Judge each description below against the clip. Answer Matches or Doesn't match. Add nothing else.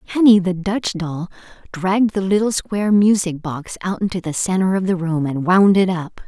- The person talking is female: Matches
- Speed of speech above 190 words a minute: Matches